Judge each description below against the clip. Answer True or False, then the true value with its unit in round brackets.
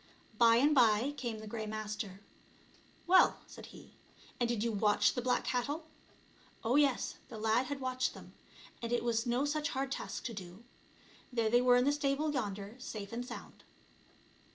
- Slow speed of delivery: False (175 wpm)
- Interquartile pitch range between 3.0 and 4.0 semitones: True (3.4 semitones)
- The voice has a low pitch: False (240 Hz)